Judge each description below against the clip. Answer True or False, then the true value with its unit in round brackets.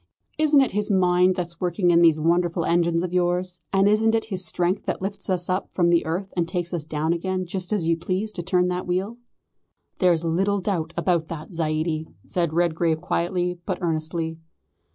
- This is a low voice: False (175 Hz)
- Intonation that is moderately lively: False (1.9 semitones)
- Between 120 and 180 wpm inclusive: False (195 wpm)